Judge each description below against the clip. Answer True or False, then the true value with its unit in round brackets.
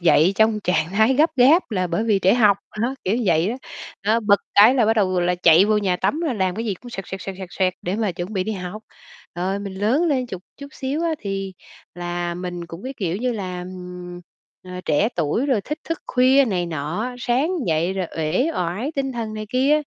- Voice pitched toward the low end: False (200 Hz)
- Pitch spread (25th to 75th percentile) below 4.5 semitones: False (5.2 semitones)